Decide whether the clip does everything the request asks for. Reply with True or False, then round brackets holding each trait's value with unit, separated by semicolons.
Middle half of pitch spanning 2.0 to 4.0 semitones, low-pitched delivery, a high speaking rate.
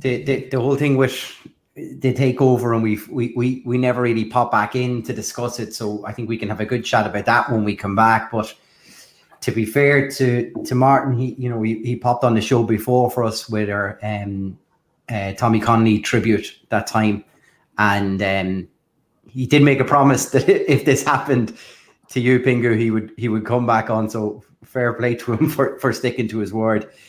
True (2.9 semitones; 120 Hz; 215 wpm)